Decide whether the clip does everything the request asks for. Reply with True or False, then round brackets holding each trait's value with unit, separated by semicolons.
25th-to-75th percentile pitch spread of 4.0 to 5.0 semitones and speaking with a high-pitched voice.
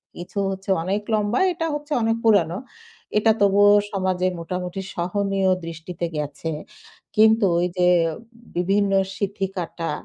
False (2.6 semitones; 195 Hz)